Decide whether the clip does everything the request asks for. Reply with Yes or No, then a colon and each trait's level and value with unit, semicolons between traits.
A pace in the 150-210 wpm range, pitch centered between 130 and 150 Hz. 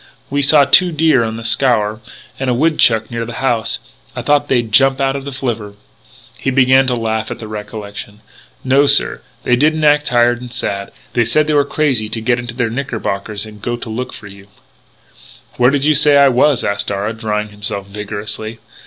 No: fast, 205 wpm; low, 120 Hz